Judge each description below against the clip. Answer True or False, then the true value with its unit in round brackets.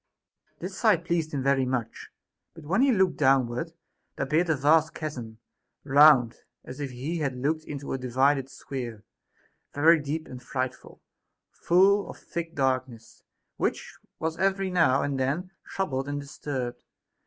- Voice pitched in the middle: True (145 Hz)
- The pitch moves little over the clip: False (4.1 semitones)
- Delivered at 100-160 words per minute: True (150 wpm)